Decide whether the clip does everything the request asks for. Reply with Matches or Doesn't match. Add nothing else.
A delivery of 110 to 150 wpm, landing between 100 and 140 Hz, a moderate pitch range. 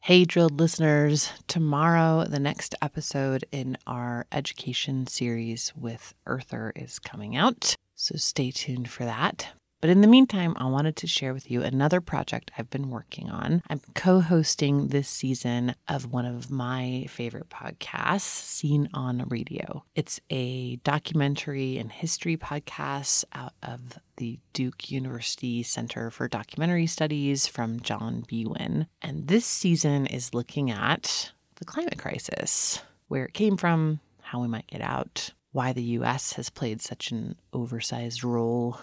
Matches